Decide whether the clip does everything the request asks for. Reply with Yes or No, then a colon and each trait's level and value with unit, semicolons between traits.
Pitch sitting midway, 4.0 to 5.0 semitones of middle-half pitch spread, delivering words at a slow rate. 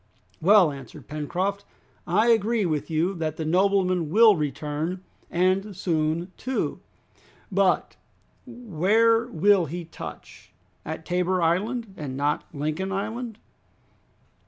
Yes: medium, 180 Hz; average, 4.5 semitones; slow, 115 wpm